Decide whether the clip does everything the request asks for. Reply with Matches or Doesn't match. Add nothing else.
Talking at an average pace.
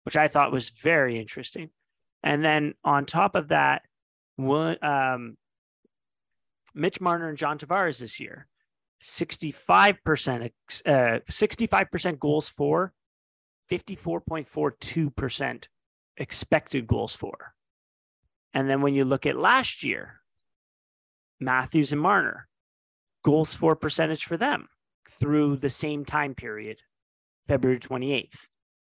Doesn't match